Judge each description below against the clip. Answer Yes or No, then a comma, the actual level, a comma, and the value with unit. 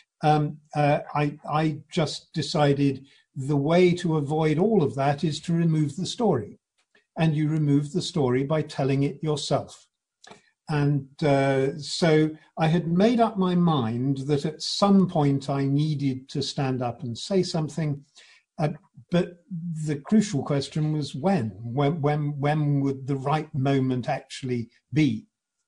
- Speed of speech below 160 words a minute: Yes, average, 150 wpm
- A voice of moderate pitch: Yes, medium, 150 Hz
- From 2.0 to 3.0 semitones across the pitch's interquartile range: Yes, narrow, 2.6 semitones